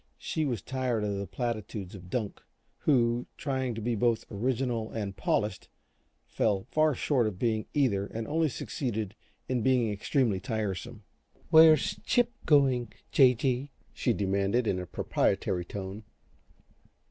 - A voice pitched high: No, low, 115 Hz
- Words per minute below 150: Yes, average, 140 wpm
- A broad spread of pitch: No, average, 4.3 semitones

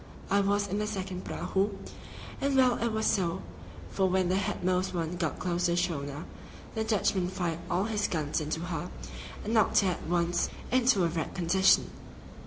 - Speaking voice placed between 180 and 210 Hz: Yes, medium, 185 Hz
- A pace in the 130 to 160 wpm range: No, average, 185 wpm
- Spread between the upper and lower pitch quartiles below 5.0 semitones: Yes, average, 2.9 semitones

